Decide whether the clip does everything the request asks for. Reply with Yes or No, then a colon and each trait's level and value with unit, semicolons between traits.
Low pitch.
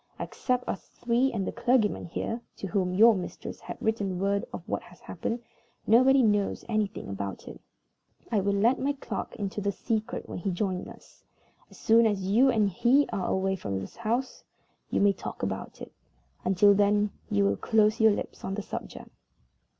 No: high, 205 Hz